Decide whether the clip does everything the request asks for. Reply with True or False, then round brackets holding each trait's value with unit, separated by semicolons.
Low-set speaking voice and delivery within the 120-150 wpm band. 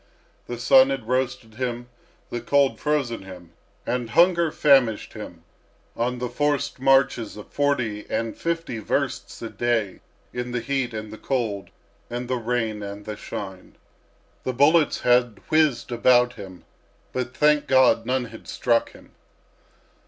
True (120 Hz; 145 wpm)